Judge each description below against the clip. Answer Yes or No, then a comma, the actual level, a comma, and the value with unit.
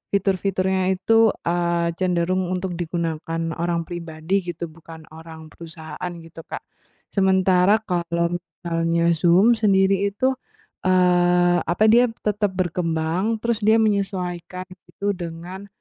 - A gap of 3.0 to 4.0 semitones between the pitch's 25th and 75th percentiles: No, narrow, 2.5 semitones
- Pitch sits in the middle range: Yes, medium, 180 Hz